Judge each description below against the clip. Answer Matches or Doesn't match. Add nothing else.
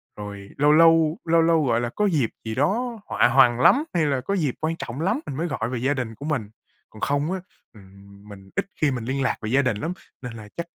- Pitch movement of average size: Doesn't match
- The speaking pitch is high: Doesn't match